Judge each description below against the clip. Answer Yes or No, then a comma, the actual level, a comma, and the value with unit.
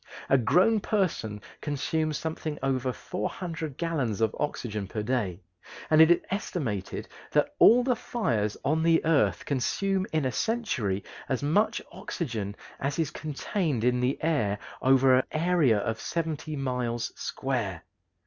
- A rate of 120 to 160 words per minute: Yes, average, 140 wpm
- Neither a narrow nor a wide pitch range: No, wide, 5.9 semitones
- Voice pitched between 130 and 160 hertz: Yes, medium, 140 Hz